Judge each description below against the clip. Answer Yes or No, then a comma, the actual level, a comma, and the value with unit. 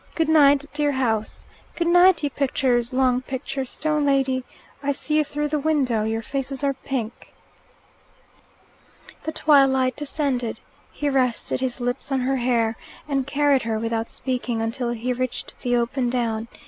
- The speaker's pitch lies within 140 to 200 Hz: No, very high, 265 Hz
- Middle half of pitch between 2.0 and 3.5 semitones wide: Yes, average, 2.9 semitones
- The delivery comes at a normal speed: Yes, average, 150 wpm